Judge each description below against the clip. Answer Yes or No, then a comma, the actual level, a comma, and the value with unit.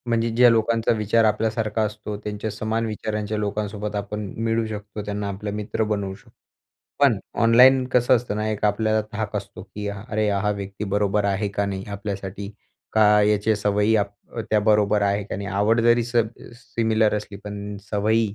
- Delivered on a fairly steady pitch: Yes, narrow, 1.5 semitones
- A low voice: Yes, low, 105 Hz